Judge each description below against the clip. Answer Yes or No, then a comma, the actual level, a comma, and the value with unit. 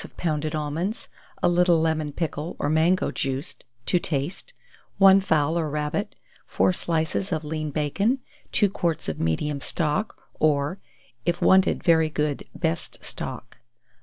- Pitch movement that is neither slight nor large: Yes, average, 3.0 semitones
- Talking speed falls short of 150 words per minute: Yes, average, 140 wpm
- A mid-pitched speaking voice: Yes, medium, 160 Hz